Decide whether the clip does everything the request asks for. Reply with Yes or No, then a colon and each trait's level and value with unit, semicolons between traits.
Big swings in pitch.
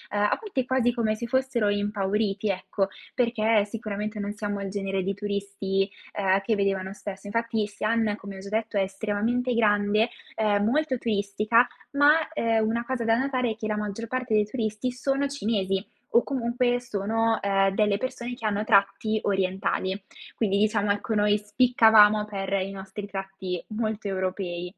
No: average, 2.7 semitones